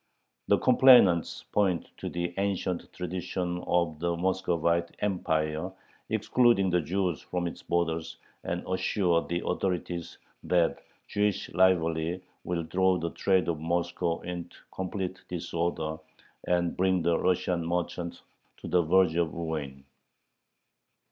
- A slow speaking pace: Yes, slow, 120 wpm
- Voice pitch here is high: No, very low, 85 Hz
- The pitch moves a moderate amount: No, narrow, 1.7 semitones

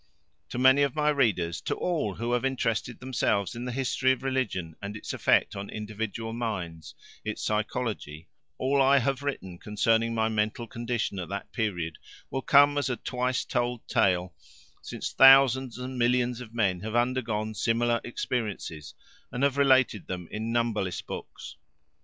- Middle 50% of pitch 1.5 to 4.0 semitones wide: Yes, average, 3.7 semitones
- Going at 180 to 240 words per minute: No, average, 160 wpm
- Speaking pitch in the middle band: No, low, 115 Hz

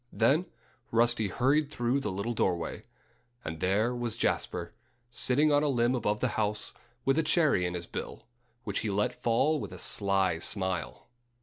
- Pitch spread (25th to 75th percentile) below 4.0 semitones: No, average, 5.2 semitones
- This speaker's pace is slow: No, average, 170 wpm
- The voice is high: No, low, 115 Hz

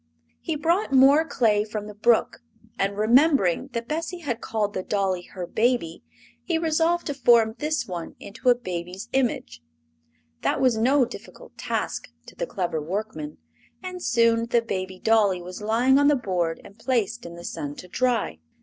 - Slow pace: No, average, 170 wpm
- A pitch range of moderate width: No, wide, 5.9 semitones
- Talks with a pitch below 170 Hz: No, high, 225 Hz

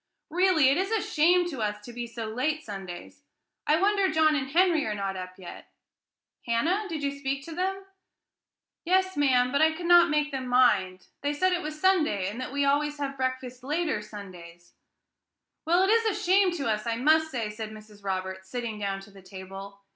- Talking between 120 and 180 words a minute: No, average, 200 wpm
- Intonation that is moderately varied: No, wide, 7.4 semitones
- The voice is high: Yes, very high, 270 Hz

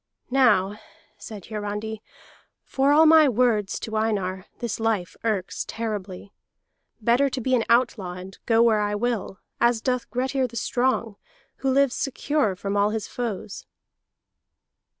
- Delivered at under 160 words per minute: Yes, average, 140 wpm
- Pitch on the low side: No, high, 225 Hz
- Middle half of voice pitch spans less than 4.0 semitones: Yes, average, 3.5 semitones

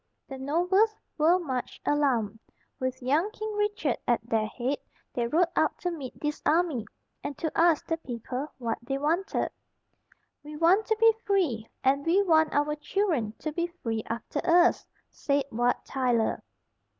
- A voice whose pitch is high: Yes, very high, 295 Hz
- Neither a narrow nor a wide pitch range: No, wide, 5.7 semitones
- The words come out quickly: No, average, 160 wpm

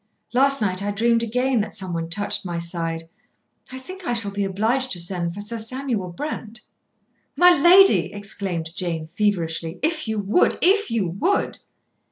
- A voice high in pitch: Yes, high, 205 Hz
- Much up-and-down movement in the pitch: Yes, wide, 6.4 semitones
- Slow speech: No, average, 165 wpm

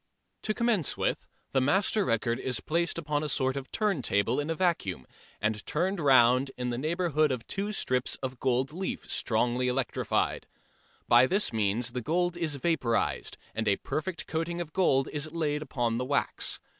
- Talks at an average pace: Yes, average, 170 wpm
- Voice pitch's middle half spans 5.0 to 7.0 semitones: Yes, wide, 5.4 semitones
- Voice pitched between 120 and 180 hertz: Yes, medium, 140 Hz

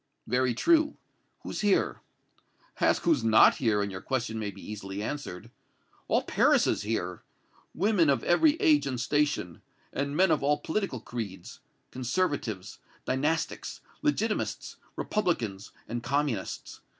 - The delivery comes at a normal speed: No, slow, 130 wpm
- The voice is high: No, low, 130 Hz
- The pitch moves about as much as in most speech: No, wide, 7.6 semitones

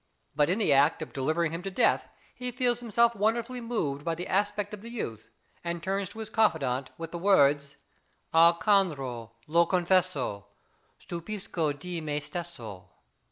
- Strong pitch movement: Yes, wide, 6.0 semitones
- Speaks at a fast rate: No, average, 160 wpm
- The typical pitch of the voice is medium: Yes, medium, 170 Hz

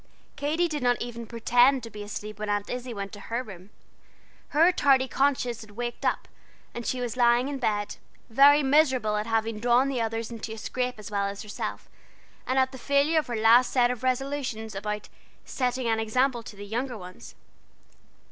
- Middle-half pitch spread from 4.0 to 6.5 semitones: No, average, 3.3 semitones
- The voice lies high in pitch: Yes, high, 240 Hz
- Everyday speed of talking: Yes, average, 195 wpm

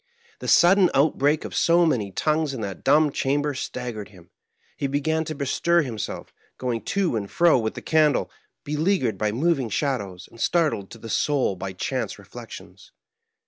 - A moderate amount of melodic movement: No, wide, 6.2 semitones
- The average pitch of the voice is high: No, medium, 140 Hz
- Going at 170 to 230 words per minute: Yes, average, 175 wpm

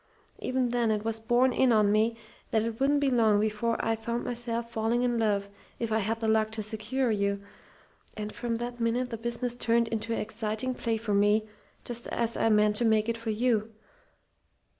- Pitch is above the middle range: Yes, high, 225 Hz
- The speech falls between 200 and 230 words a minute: Yes, fast, 205 wpm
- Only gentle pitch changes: Yes, narrow, 1.8 semitones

